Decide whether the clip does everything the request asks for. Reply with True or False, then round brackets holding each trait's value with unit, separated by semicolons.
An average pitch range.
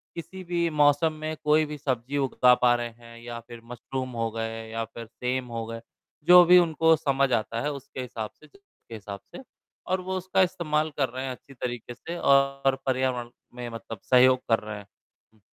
True (4.6 semitones)